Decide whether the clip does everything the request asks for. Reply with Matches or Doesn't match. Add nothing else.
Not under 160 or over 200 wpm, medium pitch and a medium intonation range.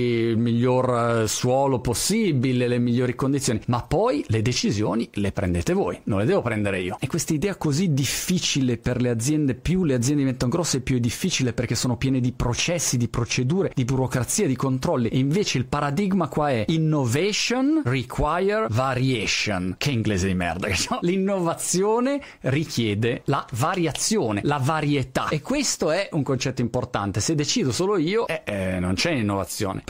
Doesn't match